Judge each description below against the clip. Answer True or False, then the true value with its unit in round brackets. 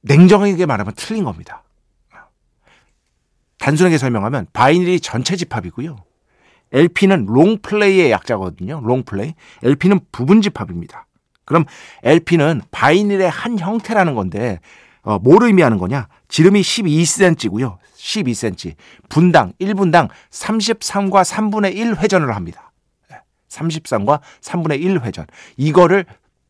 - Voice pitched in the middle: True (165 Hz)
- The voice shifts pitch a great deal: True (8.3 semitones)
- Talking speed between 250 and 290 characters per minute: True (255 characters per minute)